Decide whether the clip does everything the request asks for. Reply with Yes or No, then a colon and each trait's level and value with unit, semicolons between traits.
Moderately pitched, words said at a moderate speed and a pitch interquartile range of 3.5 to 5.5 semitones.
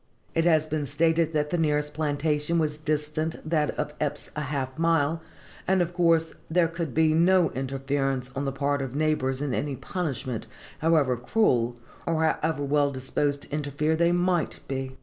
No: medium, 150 Hz; average, 180 wpm; average, 2.7 semitones